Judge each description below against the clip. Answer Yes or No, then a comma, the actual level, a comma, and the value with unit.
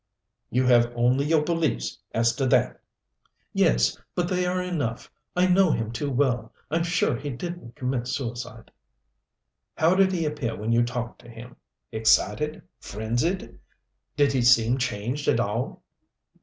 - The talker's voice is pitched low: Yes, low, 125 Hz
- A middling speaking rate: Yes, average, 150 wpm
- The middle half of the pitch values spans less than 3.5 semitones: No, average, 5.2 semitones